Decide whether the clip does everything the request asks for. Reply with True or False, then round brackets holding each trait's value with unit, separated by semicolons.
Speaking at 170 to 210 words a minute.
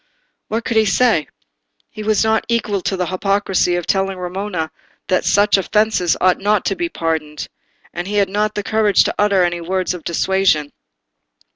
True (175 wpm)